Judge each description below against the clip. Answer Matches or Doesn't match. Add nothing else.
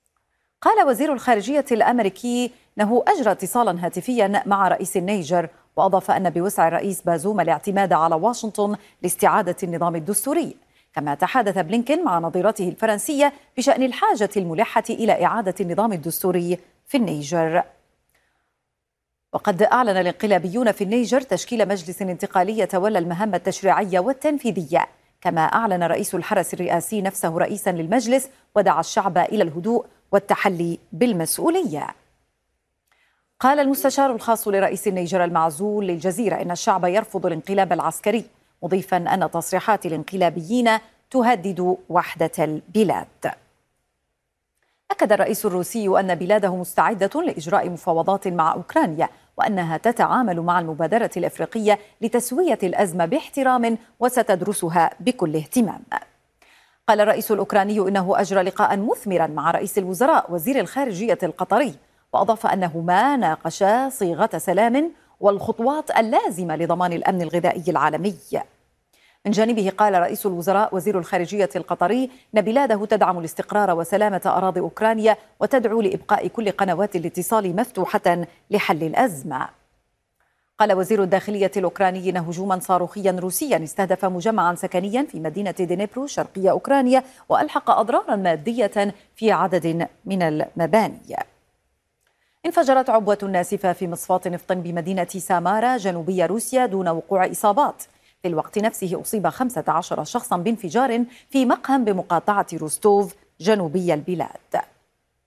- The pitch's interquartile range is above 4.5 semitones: Doesn't match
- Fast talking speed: Doesn't match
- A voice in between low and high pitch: Doesn't match